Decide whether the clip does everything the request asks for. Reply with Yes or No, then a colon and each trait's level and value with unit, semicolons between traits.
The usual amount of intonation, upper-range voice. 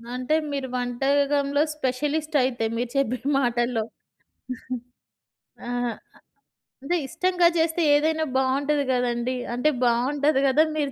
Yes: average, 3.1 semitones; very high, 270 Hz